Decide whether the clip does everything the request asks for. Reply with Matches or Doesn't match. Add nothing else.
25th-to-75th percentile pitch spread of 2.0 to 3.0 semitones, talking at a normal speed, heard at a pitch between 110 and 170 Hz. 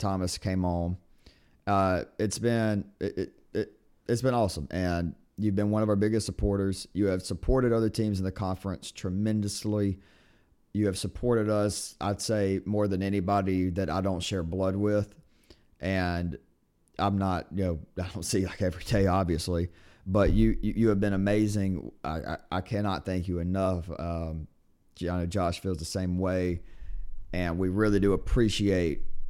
Doesn't match